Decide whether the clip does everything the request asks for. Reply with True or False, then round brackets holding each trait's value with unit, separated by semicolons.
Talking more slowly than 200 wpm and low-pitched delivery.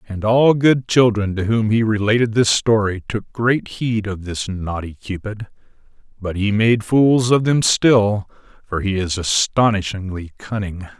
True (160 wpm; 110 Hz)